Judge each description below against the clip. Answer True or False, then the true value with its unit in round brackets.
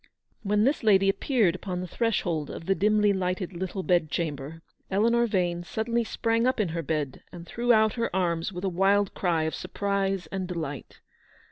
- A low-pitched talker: False (190 Hz)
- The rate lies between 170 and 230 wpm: True (175 wpm)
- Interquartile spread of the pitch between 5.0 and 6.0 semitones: False (3.7 semitones)